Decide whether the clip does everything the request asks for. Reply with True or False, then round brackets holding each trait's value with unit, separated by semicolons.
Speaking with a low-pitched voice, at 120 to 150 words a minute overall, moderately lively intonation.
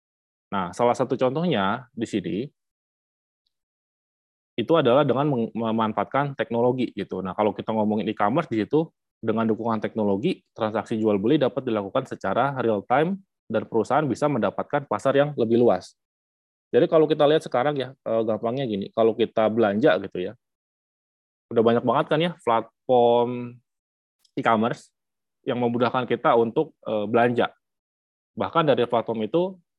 True (115 Hz; 135 wpm; 3.5 semitones)